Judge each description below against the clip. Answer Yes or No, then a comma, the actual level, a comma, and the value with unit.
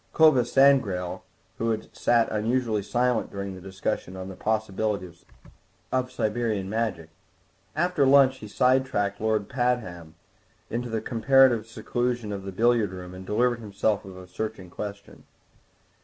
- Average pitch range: Yes, average, 4.0 semitones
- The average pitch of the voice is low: Yes, low, 110 Hz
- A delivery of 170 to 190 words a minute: No, average, 140 wpm